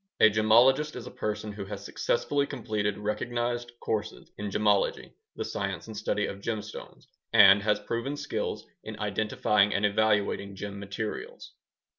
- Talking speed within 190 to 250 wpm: No, average, 145 wpm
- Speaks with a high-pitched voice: No, low, 105 Hz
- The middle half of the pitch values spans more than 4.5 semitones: No, narrow, 2.5 semitones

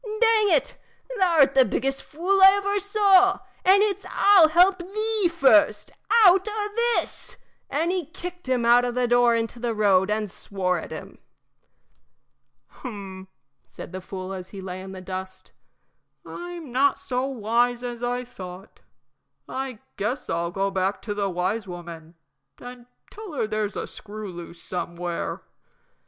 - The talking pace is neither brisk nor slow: Yes, average, 155 wpm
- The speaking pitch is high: Yes, high, 245 Hz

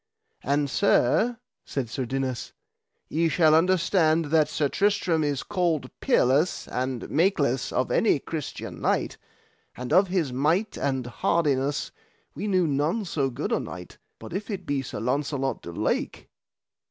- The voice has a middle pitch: Yes, medium, 150 Hz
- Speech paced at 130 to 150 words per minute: Yes, average, 145 wpm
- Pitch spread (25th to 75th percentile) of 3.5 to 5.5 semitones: Yes, average, 5.1 semitones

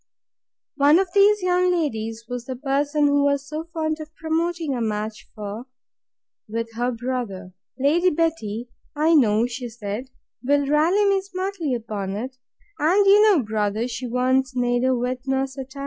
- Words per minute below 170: Yes, average, 155 wpm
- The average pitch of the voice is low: No, very high, 265 Hz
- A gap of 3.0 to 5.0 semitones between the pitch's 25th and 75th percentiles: No, wide, 5.4 semitones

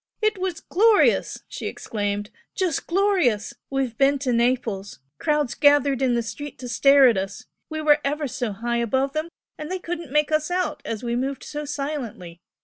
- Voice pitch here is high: Yes, very high, 275 Hz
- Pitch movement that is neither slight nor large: Yes, average, 4.5 semitones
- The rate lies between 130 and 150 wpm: No, average, 180 wpm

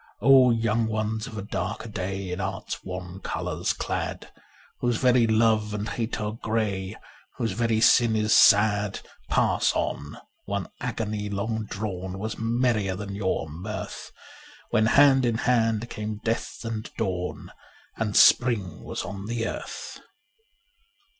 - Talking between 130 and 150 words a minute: Yes, average, 140 wpm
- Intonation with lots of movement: No, narrow, 2.4 semitones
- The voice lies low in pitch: Yes, low, 110 Hz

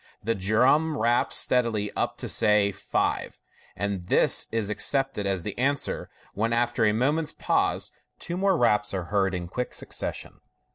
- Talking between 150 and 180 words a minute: Yes, average, 155 wpm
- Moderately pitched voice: No, low, 110 Hz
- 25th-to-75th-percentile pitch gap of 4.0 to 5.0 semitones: Yes, average, 4.3 semitones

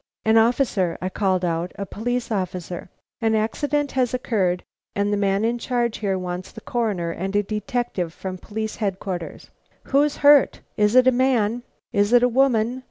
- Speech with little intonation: No, average, 4.4 semitones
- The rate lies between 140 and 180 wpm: Yes, average, 170 wpm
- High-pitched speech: Yes, high, 215 Hz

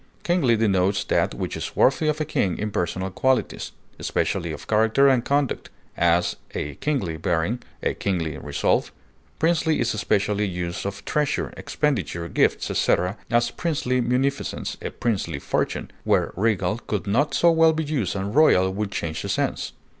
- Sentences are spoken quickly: No, average, 160 wpm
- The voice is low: Yes, low, 110 Hz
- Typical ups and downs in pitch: No, wide, 6.8 semitones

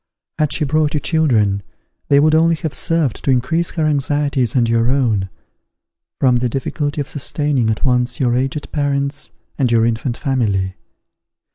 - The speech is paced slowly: No, average, 160 wpm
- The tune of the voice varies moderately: Yes, average, 3.7 semitones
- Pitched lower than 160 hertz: Yes, low, 135 Hz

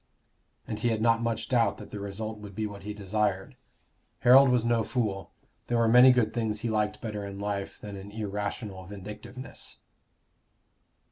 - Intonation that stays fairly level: Yes, narrow, 2.3 semitones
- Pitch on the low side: Yes, low, 105 Hz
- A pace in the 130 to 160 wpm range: No, average, 175 wpm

